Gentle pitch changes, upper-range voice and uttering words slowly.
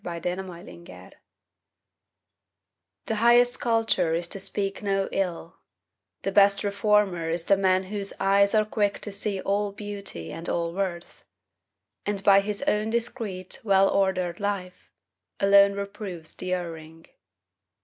Yes: narrow, 2.3 semitones; high, 195 Hz; slow, 130 wpm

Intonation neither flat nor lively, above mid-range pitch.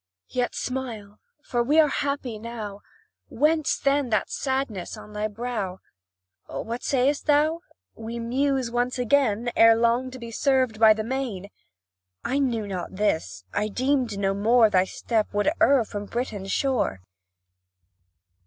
Yes: average, 3.9 semitones; high, 235 Hz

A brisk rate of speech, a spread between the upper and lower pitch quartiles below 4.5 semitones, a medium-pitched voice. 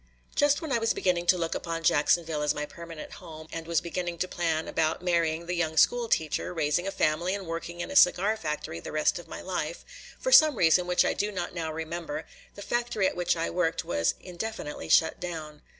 Yes: fast, 215 wpm; narrow, 2.4 semitones; medium, 170 Hz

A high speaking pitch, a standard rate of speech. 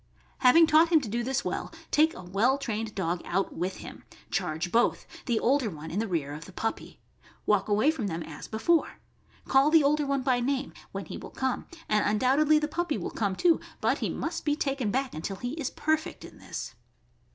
No: very high, 250 Hz; fast, 210 wpm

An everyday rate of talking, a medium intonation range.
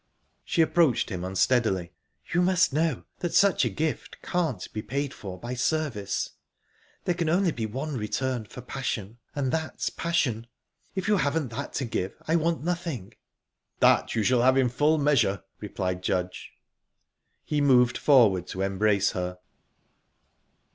No: average, 150 wpm; wide, 7.1 semitones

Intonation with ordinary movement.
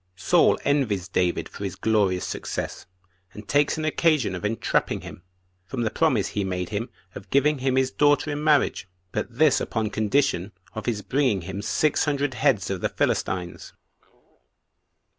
No: wide, 6.5 semitones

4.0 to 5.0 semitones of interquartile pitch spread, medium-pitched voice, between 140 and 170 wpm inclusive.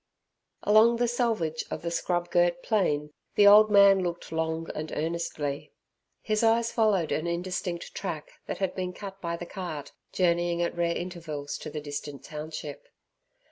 No: average, 3.6 semitones; medium, 175 Hz; average, 160 wpm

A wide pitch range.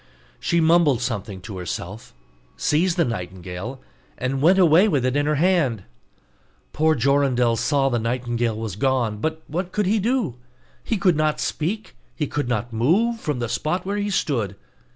Yes: wide, 6.6 semitones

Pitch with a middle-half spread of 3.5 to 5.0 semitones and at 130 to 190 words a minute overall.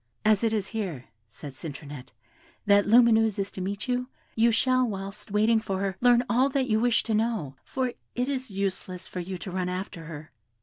No: average, 4.3 semitones; average, 200 wpm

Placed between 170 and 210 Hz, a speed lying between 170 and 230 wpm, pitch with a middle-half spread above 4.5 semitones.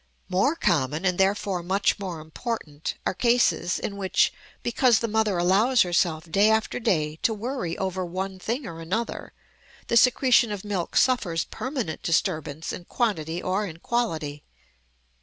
No: high, 190 Hz; average, 150 wpm; average, 5.3 semitones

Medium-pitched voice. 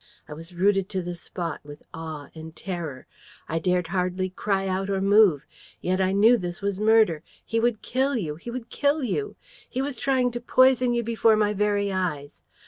No: high, 195 Hz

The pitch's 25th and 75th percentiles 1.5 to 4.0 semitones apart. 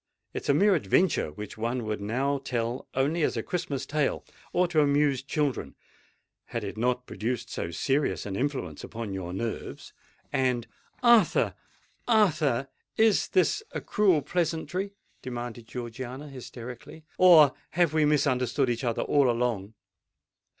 No: average, 4.6 semitones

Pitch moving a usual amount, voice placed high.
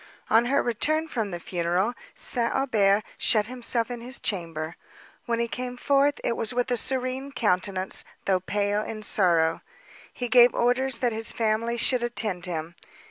Yes: average, 4.0 semitones; high, 230 Hz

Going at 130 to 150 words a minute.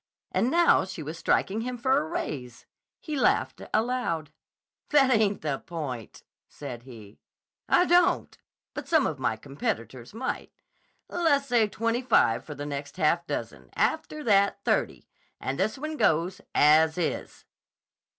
Yes: average, 140 wpm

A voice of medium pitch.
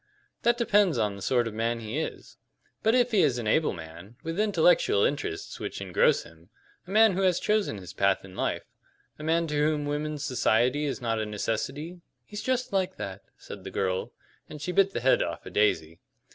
Yes: medium, 145 Hz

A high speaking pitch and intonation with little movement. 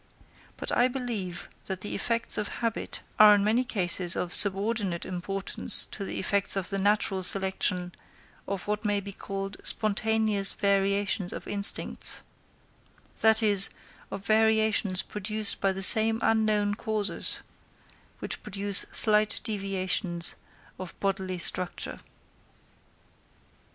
Yes: high, 200 Hz; narrow, 2.0 semitones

